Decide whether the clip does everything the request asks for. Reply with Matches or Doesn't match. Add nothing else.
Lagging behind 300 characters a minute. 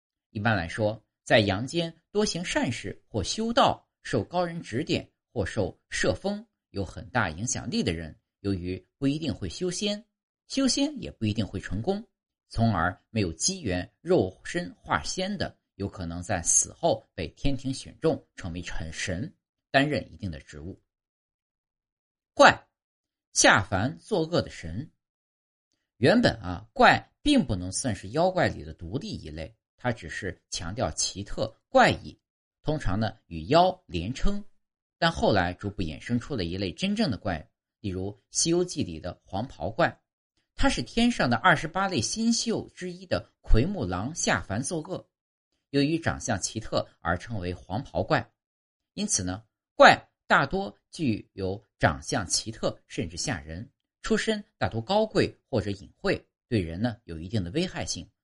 Matches